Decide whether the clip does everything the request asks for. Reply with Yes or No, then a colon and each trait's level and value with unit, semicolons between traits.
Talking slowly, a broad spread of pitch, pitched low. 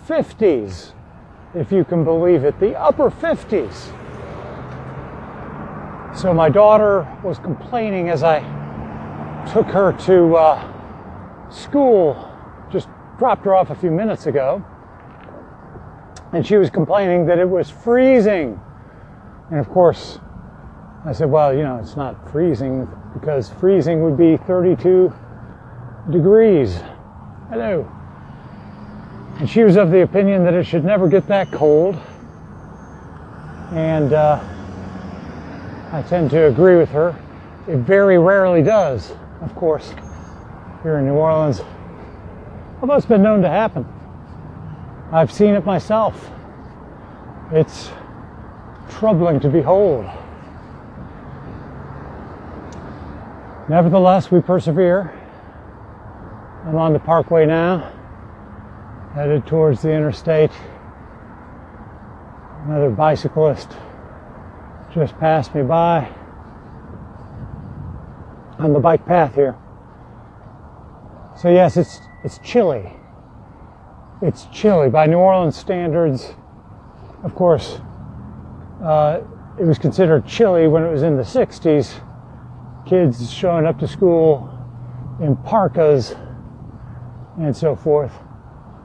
No: slow, 105 wpm; wide, 8.0 semitones; medium, 155 Hz